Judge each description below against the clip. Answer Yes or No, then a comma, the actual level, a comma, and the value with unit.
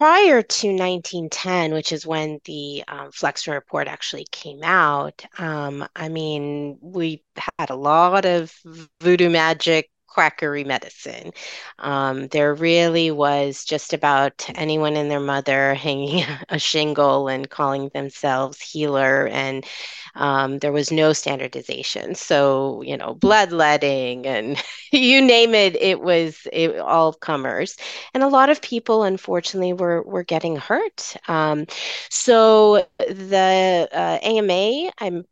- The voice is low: No, medium, 160 Hz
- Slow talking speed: Yes, slow, 130 wpm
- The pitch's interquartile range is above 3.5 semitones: Yes, average, 4.2 semitones